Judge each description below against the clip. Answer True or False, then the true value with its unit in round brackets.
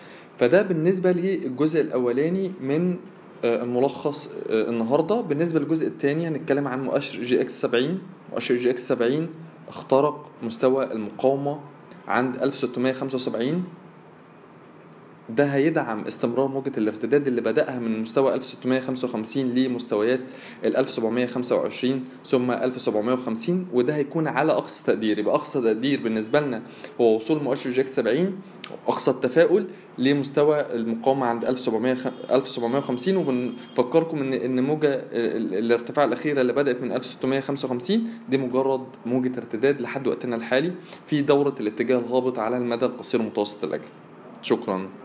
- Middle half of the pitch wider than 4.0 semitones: False (3.4 semitones)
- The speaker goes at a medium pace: True (120 wpm)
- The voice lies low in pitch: True (130 Hz)